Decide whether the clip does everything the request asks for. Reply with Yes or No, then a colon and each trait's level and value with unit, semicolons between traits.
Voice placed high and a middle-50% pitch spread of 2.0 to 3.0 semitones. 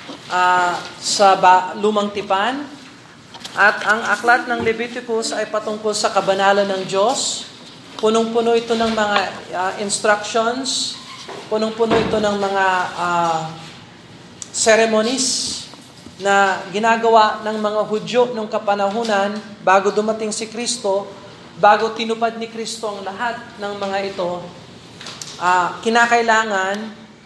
Yes: high, 215 Hz; narrow, 2.4 semitones